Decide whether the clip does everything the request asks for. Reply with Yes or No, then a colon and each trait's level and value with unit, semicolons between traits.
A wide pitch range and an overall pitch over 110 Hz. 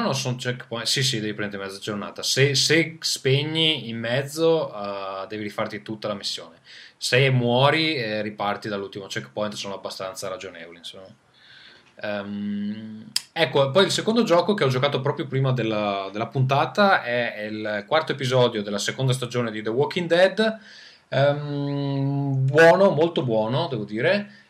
Yes: wide, 6.4 semitones; low, 130 Hz